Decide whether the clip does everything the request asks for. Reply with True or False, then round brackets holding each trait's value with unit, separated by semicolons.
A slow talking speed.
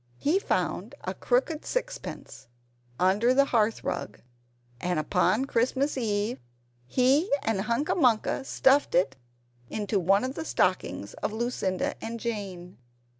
True (125 wpm)